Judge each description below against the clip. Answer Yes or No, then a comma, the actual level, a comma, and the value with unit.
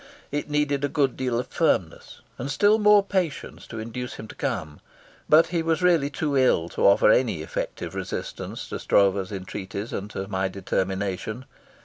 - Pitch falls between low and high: No, low, 125 Hz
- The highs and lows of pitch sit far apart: Yes, wide, 7.2 semitones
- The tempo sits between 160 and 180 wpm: Yes, average, 170 wpm